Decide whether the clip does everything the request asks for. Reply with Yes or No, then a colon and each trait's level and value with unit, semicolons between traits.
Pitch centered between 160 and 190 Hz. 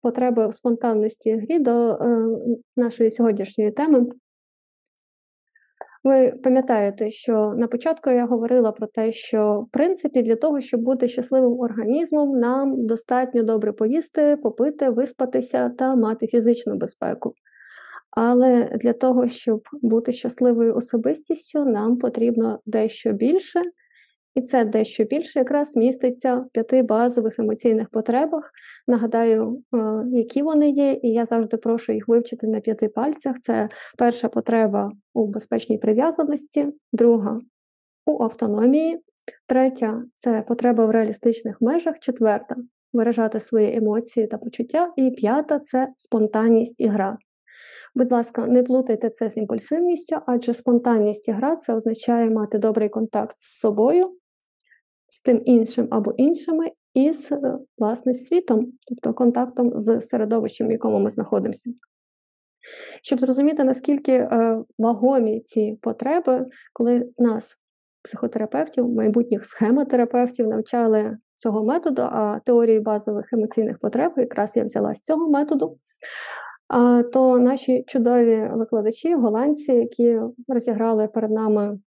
No: high, 240 Hz